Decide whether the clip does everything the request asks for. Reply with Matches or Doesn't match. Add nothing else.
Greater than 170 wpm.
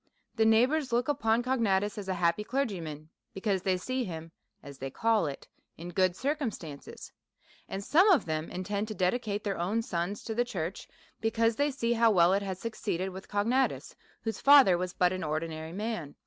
Matches